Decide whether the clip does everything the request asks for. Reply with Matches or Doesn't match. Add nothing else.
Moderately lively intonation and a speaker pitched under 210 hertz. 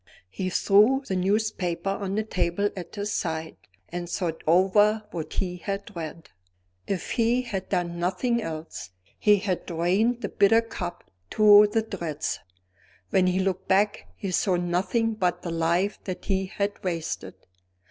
Matches